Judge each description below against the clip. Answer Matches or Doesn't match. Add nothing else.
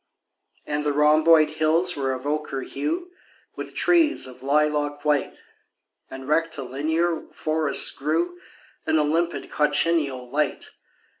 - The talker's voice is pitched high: Doesn't match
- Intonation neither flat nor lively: Doesn't match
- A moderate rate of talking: Doesn't match